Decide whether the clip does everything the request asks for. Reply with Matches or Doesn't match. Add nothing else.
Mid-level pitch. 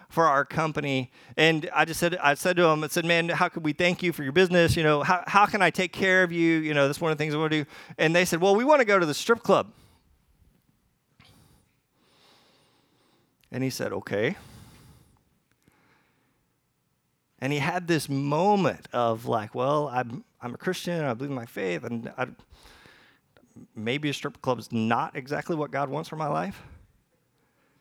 Matches